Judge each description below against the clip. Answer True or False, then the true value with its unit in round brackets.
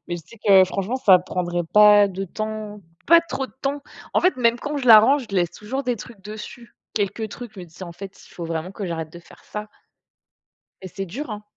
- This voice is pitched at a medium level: False (210 Hz)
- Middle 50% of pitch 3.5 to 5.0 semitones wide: True (4.3 semitones)